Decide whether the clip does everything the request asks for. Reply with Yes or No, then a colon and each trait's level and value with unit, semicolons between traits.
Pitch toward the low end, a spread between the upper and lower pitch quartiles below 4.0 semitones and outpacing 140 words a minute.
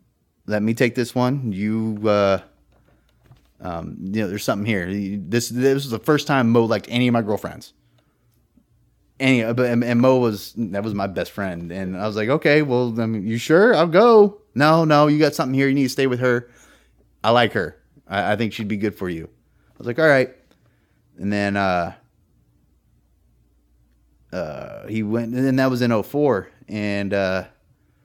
No: low, 110 Hz; average, 4.3 semitones; average, 185 wpm